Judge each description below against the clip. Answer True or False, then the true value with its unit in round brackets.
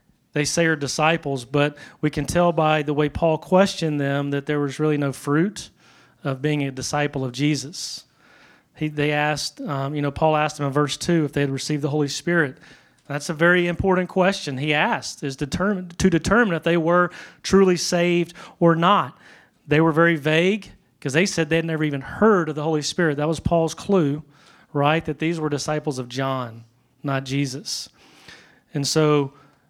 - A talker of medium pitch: True (150 Hz)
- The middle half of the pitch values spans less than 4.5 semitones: True (2.9 semitones)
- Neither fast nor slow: True (190 wpm)